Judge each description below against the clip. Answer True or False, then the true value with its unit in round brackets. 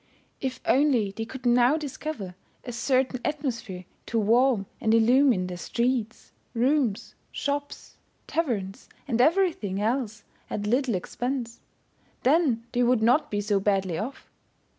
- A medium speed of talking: False (130 wpm)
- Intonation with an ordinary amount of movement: True (4.2 semitones)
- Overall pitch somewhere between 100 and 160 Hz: False (240 Hz)